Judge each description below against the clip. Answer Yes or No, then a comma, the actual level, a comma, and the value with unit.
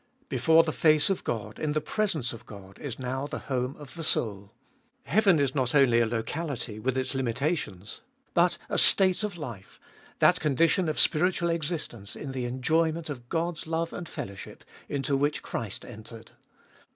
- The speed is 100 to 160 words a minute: No, average, 175 wpm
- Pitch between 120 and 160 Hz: Yes, medium, 140 Hz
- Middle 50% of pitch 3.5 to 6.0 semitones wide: Yes, wide, 5.5 semitones